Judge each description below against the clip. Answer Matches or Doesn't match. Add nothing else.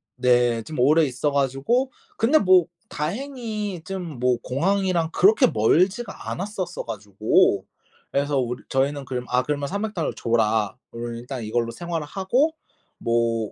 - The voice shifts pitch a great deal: Matches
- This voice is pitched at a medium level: Matches